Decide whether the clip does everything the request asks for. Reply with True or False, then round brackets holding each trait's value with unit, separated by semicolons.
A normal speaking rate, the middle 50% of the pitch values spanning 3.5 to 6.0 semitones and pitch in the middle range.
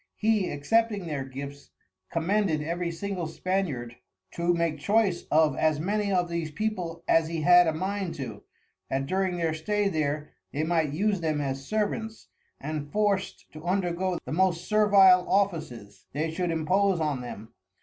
True (160 wpm; 4.3 semitones; 170 Hz)